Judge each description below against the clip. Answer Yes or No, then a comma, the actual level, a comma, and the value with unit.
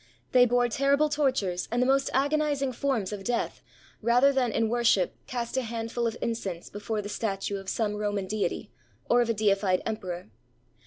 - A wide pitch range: No, average, 3.8 semitones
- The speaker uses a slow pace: No, average, 175 wpm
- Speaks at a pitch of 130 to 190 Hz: No, high, 230 Hz